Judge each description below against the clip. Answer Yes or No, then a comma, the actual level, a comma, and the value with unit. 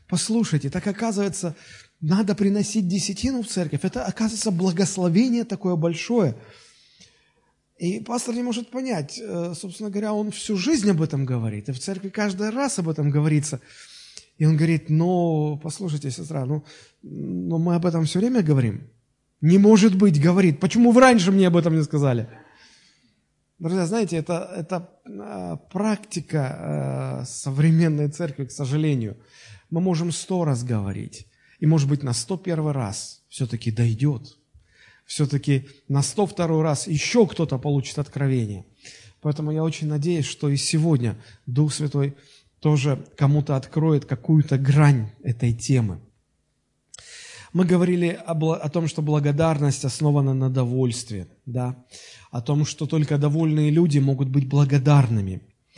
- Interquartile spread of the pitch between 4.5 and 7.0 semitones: Yes, average, 4.9 semitones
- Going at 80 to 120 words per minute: No, average, 135 wpm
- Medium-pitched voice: Yes, medium, 155 Hz